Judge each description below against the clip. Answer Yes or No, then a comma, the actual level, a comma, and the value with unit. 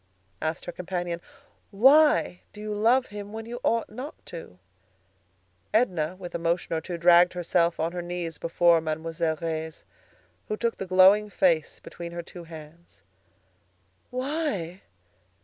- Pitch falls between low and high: Yes, medium, 175 Hz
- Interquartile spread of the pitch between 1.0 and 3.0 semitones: No, average, 4.0 semitones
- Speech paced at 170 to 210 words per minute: No, average, 145 wpm